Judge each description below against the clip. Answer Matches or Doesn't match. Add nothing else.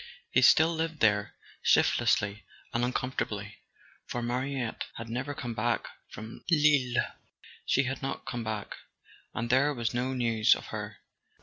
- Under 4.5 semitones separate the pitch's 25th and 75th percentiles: Matches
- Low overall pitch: Matches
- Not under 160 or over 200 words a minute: Doesn't match